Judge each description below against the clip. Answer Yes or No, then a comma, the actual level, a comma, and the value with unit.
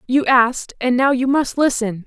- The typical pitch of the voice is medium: No, very high, 255 Hz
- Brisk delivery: No, average, 175 wpm